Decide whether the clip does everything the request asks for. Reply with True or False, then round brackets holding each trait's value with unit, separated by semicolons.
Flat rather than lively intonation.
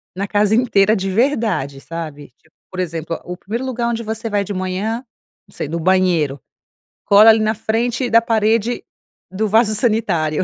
False (3.7 semitones)